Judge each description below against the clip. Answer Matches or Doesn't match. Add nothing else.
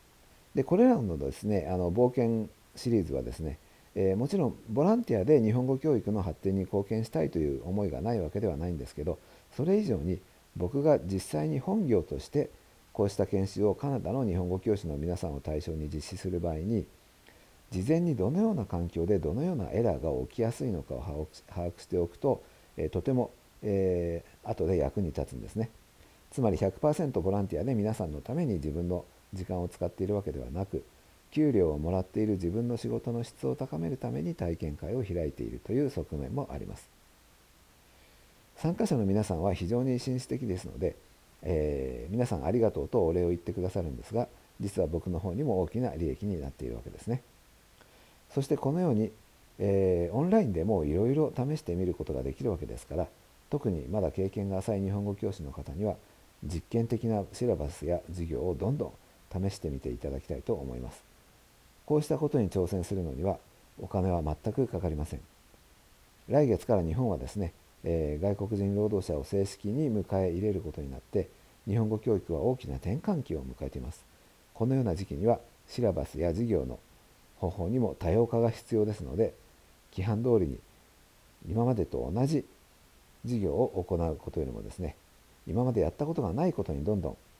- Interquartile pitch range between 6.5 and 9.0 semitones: Doesn't match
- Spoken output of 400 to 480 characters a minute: Doesn't match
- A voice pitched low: Matches